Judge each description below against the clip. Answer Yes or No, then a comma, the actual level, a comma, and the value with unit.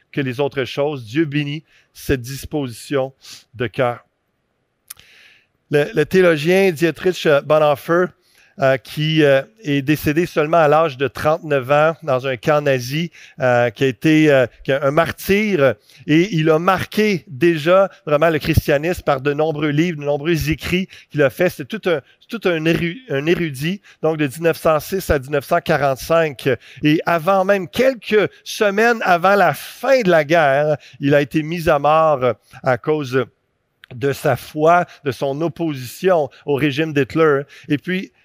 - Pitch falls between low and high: Yes, medium, 155 Hz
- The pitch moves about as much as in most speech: Yes, average, 3.6 semitones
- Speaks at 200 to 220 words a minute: No, slow, 145 wpm